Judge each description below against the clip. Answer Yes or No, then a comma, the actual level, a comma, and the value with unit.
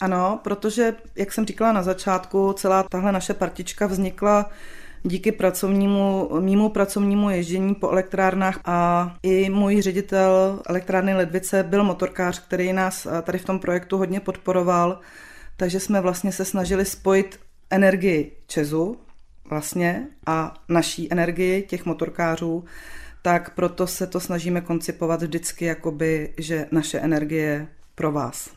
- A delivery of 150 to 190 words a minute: No, average, 130 wpm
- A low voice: No, medium, 185 Hz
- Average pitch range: No, narrow, 2.1 semitones